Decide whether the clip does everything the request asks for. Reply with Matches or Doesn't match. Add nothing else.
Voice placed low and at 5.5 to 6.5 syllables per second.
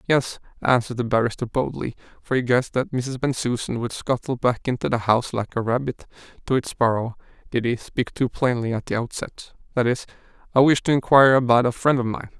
Matches